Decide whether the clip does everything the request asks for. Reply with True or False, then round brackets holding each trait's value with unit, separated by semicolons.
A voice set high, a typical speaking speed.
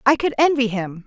False (245 Hz; 225 wpm)